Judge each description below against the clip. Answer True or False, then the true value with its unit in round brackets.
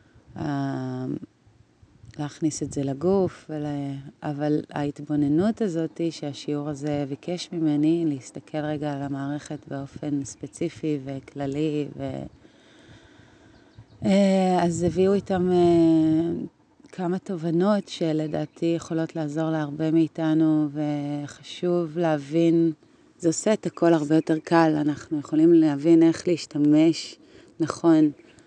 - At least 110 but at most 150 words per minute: False (100 wpm)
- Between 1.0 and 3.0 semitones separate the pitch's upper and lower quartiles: True (2.5 semitones)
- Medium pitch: True (155 Hz)